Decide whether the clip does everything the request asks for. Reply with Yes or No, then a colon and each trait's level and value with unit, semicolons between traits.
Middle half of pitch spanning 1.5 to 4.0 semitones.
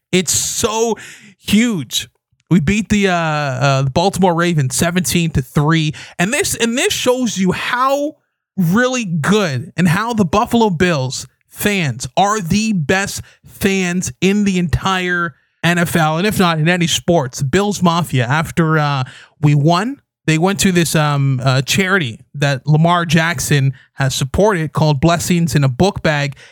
No: average, 5.1 semitones